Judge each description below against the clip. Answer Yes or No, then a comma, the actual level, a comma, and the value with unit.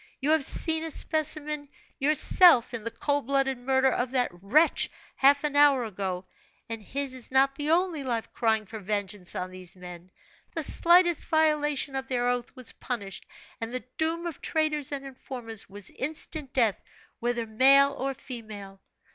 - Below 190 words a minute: Yes, average, 165 wpm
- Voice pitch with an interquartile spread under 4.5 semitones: No, average, 4.8 semitones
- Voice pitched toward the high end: Yes, very high, 265 Hz